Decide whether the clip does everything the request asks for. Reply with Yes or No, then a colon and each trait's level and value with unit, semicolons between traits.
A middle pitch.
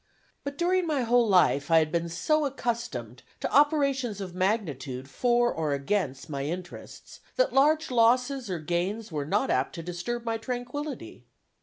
No: high, 225 Hz